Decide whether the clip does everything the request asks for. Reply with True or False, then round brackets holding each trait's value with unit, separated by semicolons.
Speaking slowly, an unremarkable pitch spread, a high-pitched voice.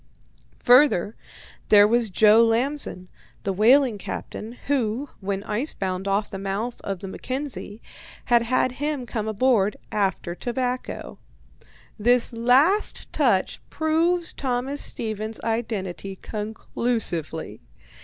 True (110 wpm; 4.0 semitones; 225 Hz)